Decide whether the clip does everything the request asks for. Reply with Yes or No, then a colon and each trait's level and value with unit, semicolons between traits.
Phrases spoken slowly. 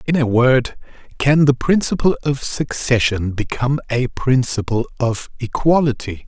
Yes: slow, 125 wpm